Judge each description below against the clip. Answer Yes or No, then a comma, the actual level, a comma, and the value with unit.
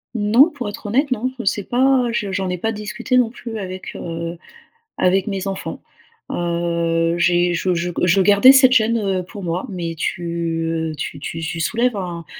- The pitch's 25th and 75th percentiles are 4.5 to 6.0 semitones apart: Yes, average, 5.0 semitones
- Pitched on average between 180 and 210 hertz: Yes, high, 190 Hz